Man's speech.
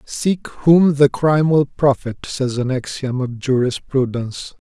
Yes: male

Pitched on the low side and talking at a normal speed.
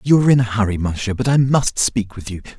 No: low, 115 Hz; fast, 280 wpm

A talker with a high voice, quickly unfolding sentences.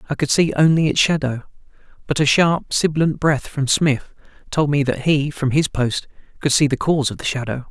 No: medium, 145 Hz; fast, 210 wpm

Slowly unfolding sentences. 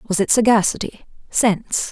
Yes: slow, 95 wpm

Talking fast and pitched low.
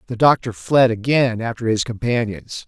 No: average, 155 wpm; low, 120 Hz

